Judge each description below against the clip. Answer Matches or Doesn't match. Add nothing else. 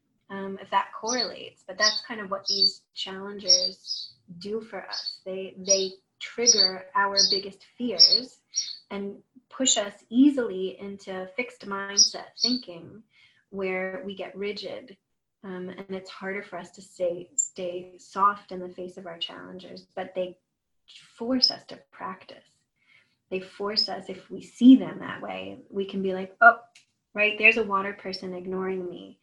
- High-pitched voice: Matches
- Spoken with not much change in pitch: Matches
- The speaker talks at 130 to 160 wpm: Matches